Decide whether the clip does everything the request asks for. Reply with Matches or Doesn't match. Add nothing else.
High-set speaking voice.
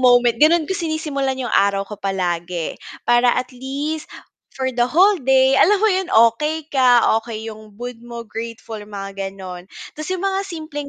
Matches